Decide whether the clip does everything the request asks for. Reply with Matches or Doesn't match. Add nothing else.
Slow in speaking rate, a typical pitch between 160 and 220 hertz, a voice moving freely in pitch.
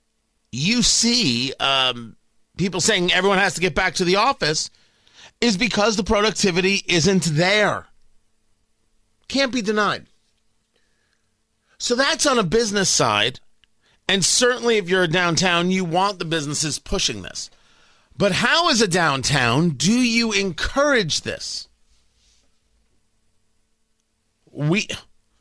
Matches